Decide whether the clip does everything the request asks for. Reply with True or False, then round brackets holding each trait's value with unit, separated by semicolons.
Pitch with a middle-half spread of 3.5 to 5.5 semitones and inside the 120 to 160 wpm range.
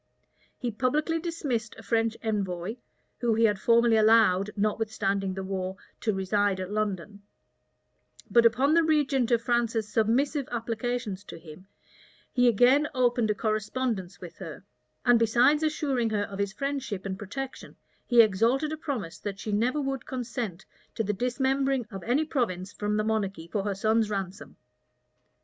True (3.9 semitones; 155 wpm)